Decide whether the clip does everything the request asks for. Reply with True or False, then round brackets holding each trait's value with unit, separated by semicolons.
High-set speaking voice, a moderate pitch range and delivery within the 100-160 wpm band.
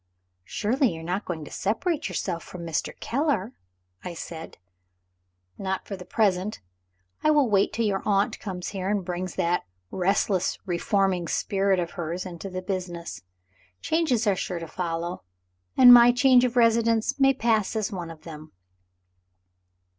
True (195 Hz; 4.6 semitones; 155 wpm)